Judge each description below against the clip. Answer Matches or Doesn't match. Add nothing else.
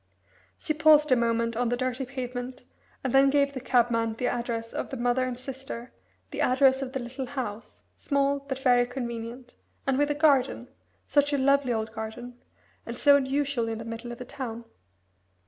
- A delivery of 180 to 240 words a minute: Matches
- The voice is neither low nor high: Doesn't match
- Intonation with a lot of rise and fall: Doesn't match